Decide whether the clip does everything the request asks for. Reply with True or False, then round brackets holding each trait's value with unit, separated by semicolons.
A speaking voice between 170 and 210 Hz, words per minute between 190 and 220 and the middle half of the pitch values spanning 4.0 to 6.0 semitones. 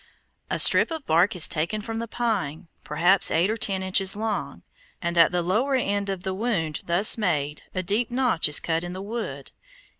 True (190 Hz; 200 wpm; 4.3 semitones)